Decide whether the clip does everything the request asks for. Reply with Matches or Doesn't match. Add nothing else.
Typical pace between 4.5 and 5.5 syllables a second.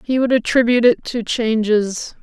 Matches